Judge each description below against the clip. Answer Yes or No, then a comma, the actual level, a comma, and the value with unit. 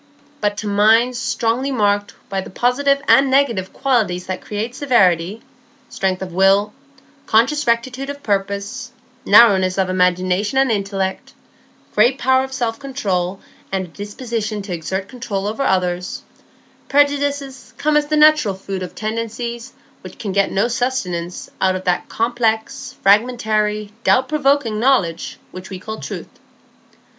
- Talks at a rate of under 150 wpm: Yes, slow, 135 wpm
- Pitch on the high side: Yes, high, 220 Hz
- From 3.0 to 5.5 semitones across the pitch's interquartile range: Yes, average, 5.2 semitones